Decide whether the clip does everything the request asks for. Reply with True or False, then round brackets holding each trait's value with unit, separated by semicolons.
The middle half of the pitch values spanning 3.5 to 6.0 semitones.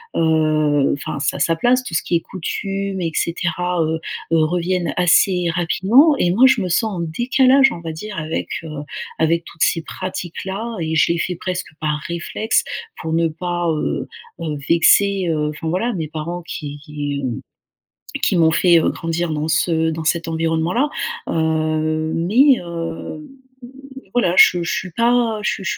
False (3.0 semitones)